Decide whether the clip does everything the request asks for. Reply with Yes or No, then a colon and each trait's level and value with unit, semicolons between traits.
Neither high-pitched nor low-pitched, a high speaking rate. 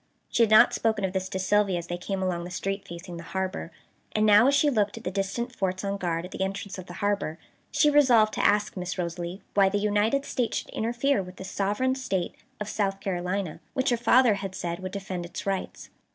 No: high, 195 Hz; fast, 230 wpm